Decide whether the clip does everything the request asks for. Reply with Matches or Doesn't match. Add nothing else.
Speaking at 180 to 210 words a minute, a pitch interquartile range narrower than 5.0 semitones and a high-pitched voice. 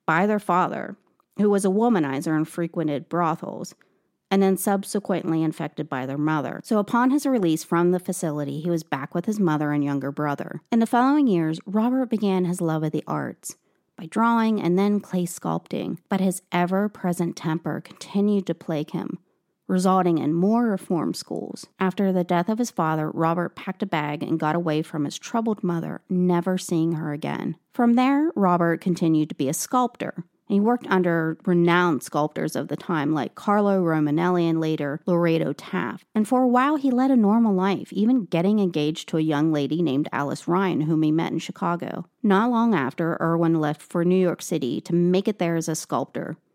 Doesn't match